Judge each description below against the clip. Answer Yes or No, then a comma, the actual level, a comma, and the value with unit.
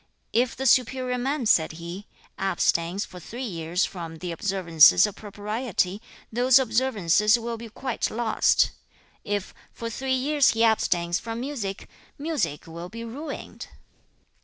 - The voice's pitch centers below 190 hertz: No, high, 220 Hz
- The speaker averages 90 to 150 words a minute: Yes, average, 140 wpm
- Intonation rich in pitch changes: Yes, wide, 5.8 semitones